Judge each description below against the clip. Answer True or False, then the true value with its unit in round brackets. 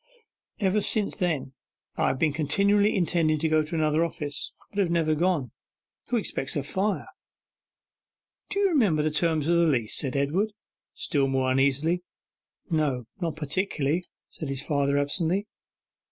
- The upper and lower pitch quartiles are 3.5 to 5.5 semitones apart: True (4.2 semitones)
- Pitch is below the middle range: False (155 Hz)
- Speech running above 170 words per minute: False (155 wpm)